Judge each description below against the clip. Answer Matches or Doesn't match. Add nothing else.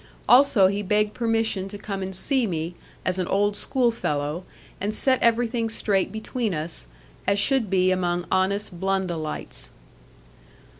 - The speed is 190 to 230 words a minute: Doesn't match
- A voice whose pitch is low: Doesn't match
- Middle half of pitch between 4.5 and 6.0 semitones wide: Doesn't match